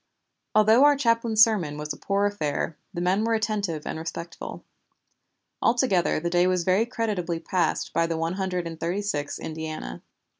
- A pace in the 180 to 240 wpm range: No, average, 165 wpm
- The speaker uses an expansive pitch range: No, average, 4.6 semitones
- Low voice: No, medium, 180 Hz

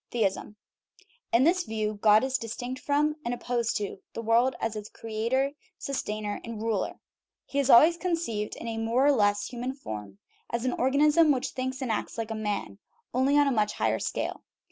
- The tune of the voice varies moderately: Yes, average, 3.8 semitones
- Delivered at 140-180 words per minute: No, average, 190 wpm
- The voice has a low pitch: No, high, 235 Hz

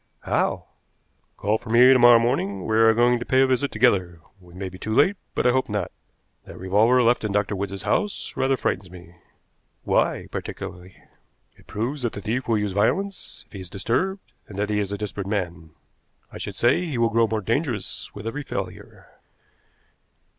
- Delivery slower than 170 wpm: No, average, 195 wpm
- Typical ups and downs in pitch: Yes, average, 3.9 semitones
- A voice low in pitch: Yes, low, 110 Hz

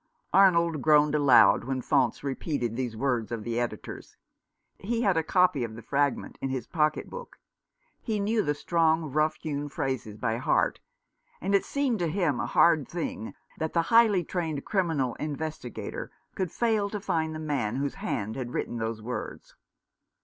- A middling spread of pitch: No, wide, 5.9 semitones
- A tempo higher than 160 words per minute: Yes, average, 170 wpm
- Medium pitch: Yes, medium, 150 Hz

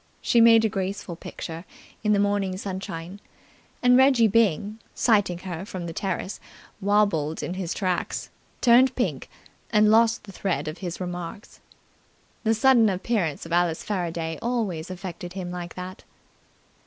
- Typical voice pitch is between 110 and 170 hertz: No, high, 190 Hz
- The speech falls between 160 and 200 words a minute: No, average, 145 wpm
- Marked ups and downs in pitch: No, average, 3.7 semitones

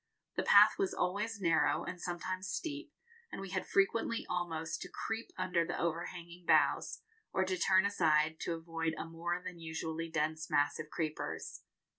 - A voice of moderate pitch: Yes, medium, 175 Hz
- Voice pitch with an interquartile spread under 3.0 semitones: Yes, narrow, 2.5 semitones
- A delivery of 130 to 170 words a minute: Yes, average, 165 wpm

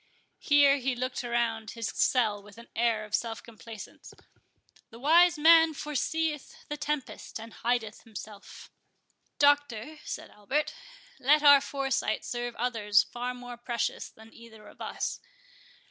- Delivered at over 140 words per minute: No, slow, 135 wpm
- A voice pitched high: Yes, high, 240 Hz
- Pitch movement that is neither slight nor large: Yes, average, 4.3 semitones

